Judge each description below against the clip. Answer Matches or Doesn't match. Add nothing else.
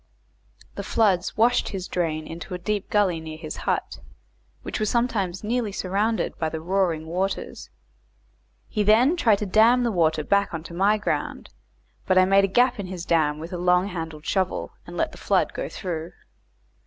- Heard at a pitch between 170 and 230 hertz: Matches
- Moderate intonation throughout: Matches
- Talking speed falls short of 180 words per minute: Doesn't match